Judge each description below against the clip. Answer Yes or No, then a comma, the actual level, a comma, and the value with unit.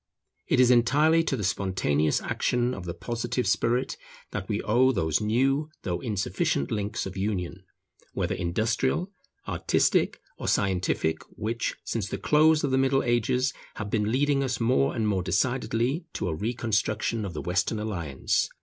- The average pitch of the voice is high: No, low, 110 Hz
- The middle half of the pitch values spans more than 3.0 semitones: Yes, average, 5.0 semitones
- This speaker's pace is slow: No, average, 160 wpm